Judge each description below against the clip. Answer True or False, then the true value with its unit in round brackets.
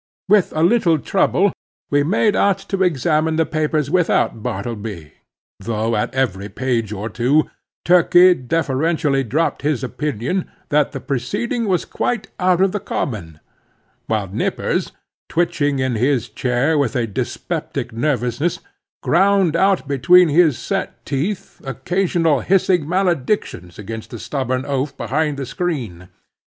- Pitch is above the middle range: False (145 Hz)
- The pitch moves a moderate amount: False (6.5 semitones)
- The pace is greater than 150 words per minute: False (135 wpm)